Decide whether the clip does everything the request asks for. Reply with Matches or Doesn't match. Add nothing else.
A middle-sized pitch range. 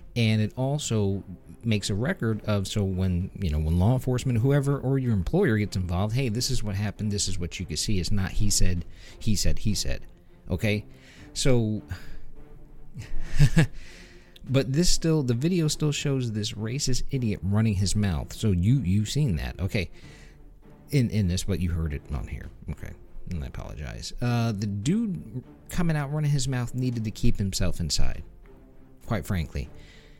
Doesn't match